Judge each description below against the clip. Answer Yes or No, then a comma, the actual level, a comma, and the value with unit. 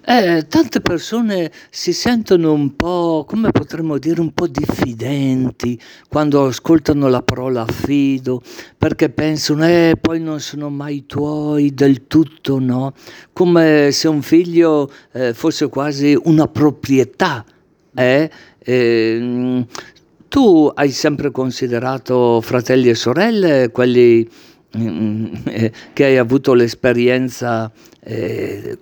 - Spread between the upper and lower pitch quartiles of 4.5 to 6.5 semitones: No, average, 4.1 semitones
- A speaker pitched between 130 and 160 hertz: Yes, medium, 140 Hz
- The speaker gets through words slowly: Yes, slow, 110 wpm